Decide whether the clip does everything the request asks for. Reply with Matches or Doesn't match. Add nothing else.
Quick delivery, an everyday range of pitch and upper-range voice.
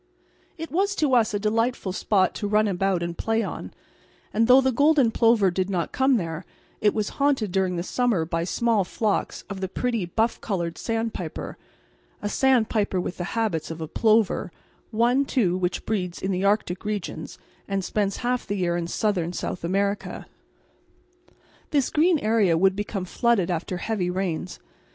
Doesn't match